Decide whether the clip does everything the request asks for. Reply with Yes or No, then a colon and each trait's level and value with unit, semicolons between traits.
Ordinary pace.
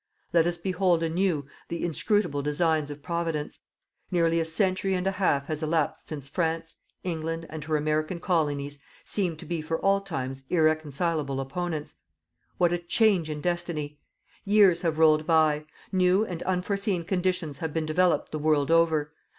Yes: average, 160 wpm